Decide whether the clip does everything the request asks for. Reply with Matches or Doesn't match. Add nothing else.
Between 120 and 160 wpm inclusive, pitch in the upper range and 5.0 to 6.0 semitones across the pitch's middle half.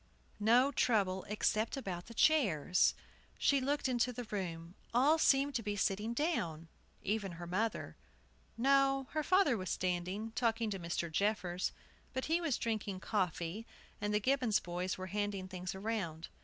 Matches